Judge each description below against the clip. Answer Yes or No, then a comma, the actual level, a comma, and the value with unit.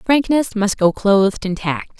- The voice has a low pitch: No, high, 210 Hz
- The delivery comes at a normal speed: Yes, average, 180 wpm